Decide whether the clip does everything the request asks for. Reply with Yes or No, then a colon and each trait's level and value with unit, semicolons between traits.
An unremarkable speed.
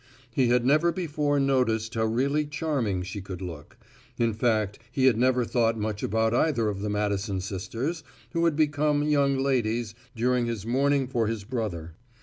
Yes: average, 170 wpm